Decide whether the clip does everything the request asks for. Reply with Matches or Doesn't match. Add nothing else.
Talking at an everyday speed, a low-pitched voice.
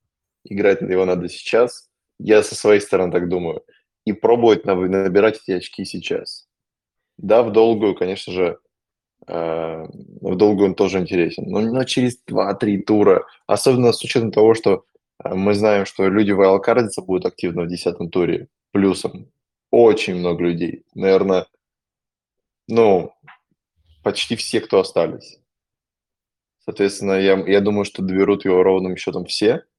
Matches